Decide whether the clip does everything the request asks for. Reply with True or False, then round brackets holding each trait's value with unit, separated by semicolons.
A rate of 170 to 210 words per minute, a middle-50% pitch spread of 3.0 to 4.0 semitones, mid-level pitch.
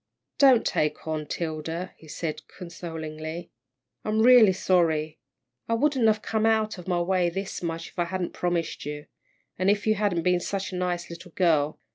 True (175 wpm; 3.7 semitones; 175 Hz)